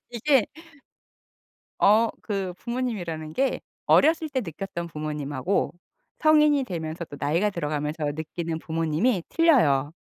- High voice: No, medium, 175 Hz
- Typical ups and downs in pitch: No, wide, 7.7 semitones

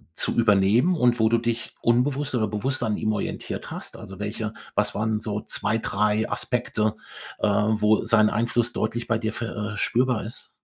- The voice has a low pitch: Yes, low, 110 Hz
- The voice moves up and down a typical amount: No, narrow, 1.9 semitones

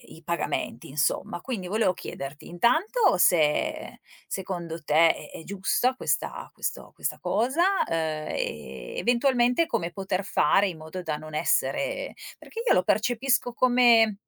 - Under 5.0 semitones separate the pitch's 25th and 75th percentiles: No, wide, 7.3 semitones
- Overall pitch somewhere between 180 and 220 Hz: Yes, medium, 185 Hz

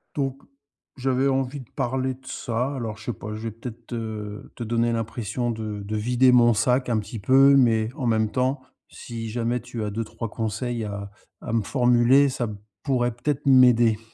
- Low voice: Yes, low, 120 Hz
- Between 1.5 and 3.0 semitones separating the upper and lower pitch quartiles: Yes, average, 2.7 semitones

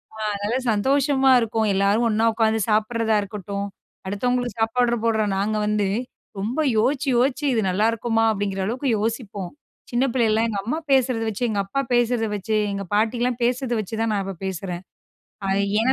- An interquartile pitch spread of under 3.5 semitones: Yes, average, 3.0 semitones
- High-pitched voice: Yes, high, 225 Hz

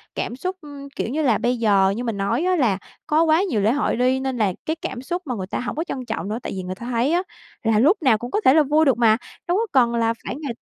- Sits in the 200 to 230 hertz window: No, very high, 250 Hz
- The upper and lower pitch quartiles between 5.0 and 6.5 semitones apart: Yes, wide, 5.4 semitones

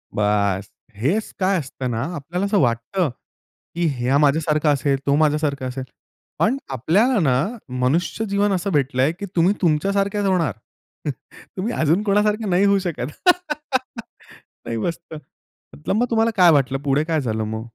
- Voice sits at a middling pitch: Yes, medium, 160 Hz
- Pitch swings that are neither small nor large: No, wide, 6.9 semitones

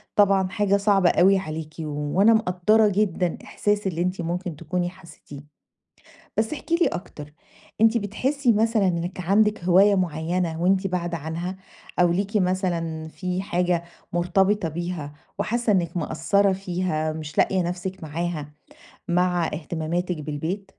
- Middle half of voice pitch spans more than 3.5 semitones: No, average, 2.9 semitones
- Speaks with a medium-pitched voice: Yes, medium, 180 Hz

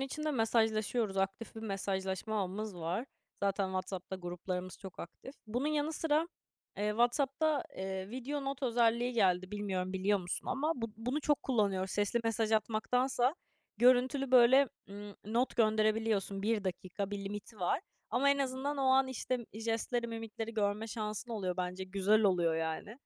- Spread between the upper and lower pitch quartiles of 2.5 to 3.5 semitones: No, average, 4.4 semitones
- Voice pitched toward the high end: Yes, high, 220 Hz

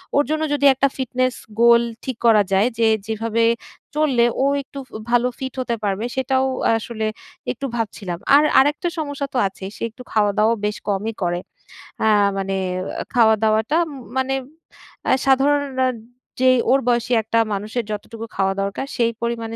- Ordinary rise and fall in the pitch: Yes, average, 3.5 semitones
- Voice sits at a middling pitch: No, high, 235 Hz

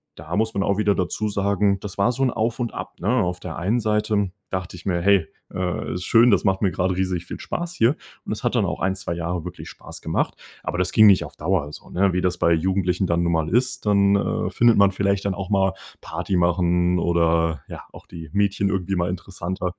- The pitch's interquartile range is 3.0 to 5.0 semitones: No, narrow, 2.5 semitones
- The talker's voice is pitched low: Yes, very low, 95 Hz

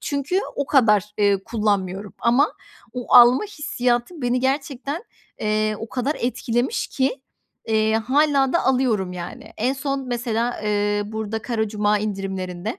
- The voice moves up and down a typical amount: Yes, average, 4.1 semitones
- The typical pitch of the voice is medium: No, high, 235 Hz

